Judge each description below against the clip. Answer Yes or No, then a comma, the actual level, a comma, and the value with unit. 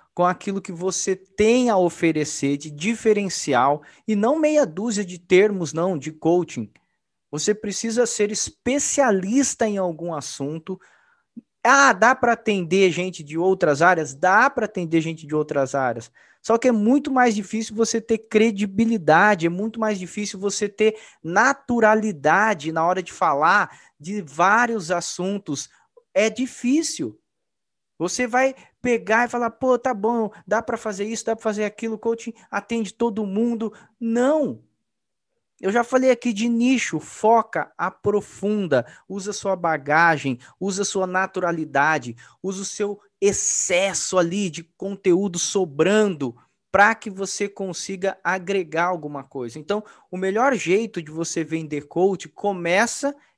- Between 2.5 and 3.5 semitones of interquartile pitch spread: No, average, 4.5 semitones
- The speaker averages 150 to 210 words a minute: No, average, 140 wpm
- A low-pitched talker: No, high, 200 Hz